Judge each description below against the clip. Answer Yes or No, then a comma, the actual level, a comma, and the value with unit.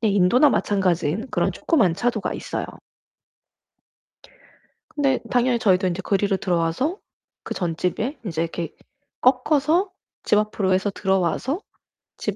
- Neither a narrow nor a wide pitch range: No, wide, 6.0 semitones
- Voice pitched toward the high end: Yes, high, 205 Hz